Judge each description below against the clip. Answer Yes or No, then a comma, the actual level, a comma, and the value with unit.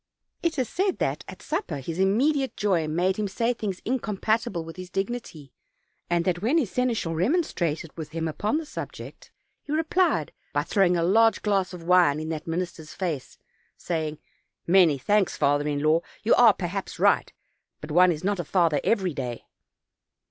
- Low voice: No, medium, 185 Hz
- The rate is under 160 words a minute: No, average, 175 wpm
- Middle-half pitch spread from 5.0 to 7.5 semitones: Yes, wide, 5.5 semitones